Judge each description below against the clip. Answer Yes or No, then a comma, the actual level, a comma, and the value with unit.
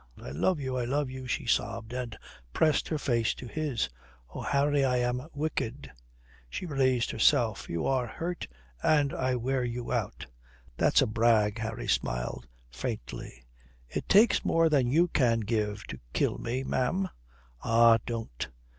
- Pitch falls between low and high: No, low, 125 Hz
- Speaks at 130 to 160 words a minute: Yes, average, 155 wpm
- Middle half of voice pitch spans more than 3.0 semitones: Yes, average, 3.7 semitones